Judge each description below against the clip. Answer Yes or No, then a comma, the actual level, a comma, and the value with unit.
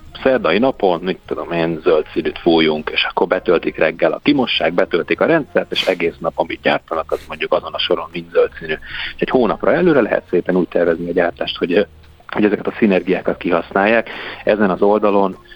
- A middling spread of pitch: Yes, average, 3.9 semitones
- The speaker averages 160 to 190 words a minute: Yes, fast, 180 wpm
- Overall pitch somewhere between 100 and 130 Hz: No, very low, 90 Hz